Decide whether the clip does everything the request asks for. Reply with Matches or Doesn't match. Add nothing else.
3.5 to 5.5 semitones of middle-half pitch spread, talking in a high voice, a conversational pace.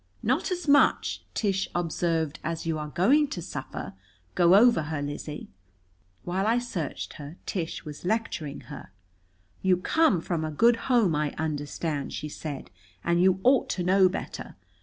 Doesn't match